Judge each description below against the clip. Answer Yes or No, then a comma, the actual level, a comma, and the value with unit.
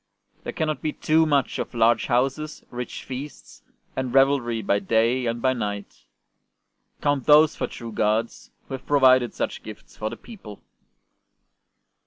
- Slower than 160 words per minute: Yes, average, 150 wpm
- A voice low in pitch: Yes, low, 130 Hz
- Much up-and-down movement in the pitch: No, average, 3.8 semitones